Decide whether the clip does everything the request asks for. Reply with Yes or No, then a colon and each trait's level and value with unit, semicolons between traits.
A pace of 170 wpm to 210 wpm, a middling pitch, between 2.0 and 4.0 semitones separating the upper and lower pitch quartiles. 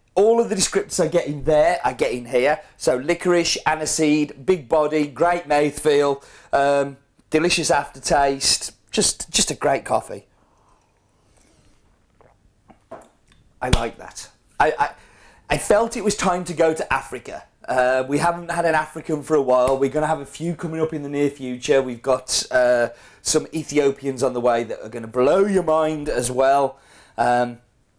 Yes: average, 175 wpm; medium, 150 Hz; average, 3.6 semitones